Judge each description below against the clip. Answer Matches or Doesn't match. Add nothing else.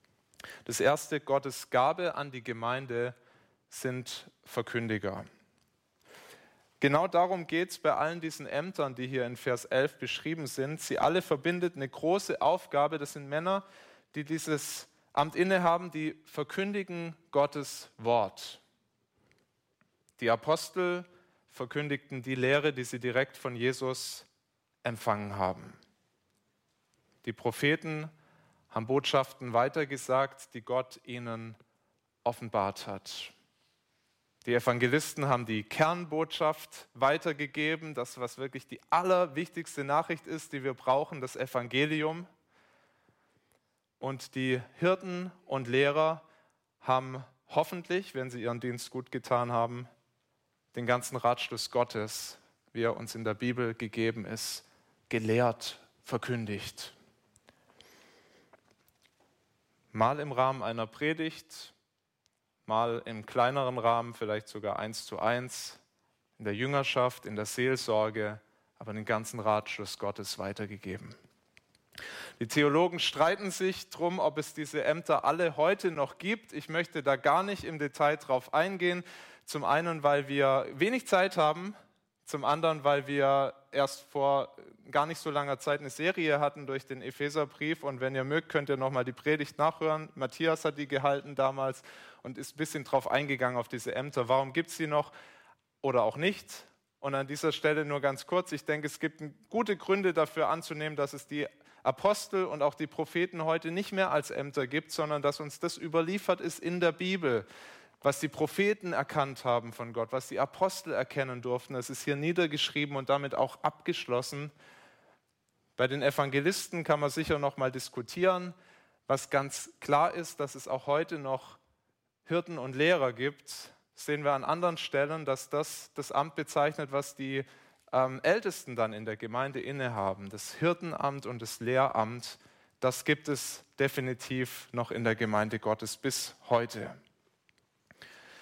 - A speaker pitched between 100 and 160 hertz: Matches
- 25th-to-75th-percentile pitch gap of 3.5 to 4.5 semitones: Matches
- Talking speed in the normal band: Matches